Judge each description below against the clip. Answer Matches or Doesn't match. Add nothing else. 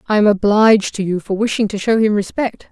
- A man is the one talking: Doesn't match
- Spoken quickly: Matches